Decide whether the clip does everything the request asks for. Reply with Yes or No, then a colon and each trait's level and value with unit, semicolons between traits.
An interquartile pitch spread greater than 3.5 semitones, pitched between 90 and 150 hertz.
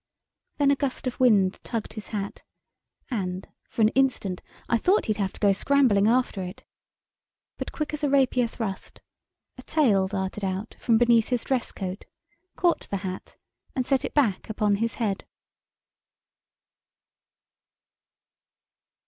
No: average, 4.6 semitones; high, 225 Hz